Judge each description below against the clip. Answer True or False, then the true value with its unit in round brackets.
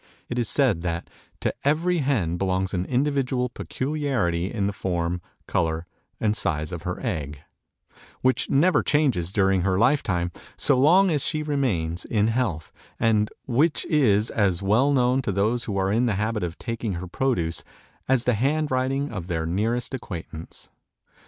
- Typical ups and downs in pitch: False (6.8 semitones)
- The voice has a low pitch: True (110 Hz)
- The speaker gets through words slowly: False (165 wpm)